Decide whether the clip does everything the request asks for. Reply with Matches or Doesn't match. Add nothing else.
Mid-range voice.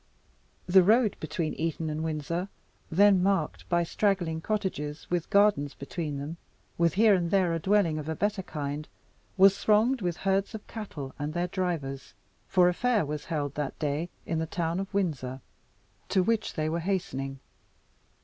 Matches